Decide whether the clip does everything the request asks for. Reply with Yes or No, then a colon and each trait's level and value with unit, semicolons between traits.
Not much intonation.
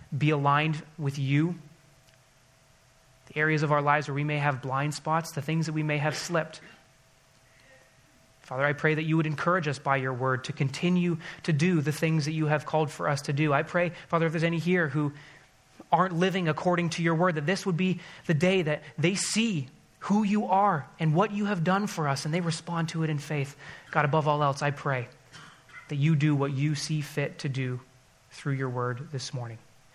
No: average, 3.2 semitones